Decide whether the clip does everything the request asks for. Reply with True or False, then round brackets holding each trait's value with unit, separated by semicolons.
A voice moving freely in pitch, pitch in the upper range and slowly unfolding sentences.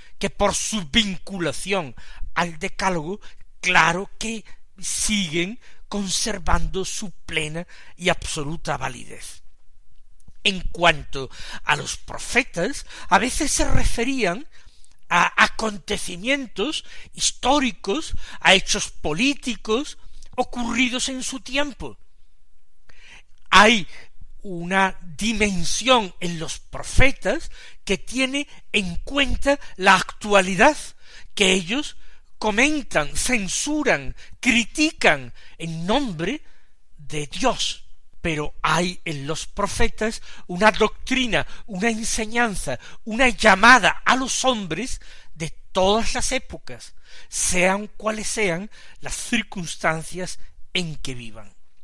True (6.0 semitones; 200 Hz; 95 wpm)